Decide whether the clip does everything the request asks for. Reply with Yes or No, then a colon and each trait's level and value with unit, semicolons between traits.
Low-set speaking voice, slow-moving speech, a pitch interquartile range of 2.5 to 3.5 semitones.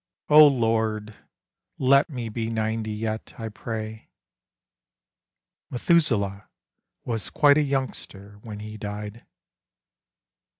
Yes: low, 110 Hz; slow, 95 wpm; average, 3.1 semitones